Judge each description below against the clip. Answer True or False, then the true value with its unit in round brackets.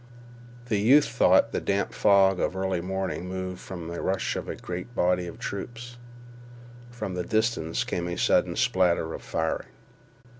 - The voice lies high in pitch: False (95 Hz)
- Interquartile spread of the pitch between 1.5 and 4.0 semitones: True (3.4 semitones)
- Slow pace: False (160 wpm)